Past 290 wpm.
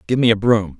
Yes: fast, 300 wpm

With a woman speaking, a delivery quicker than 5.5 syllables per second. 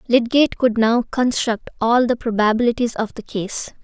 No: female; 5.0 syllables/s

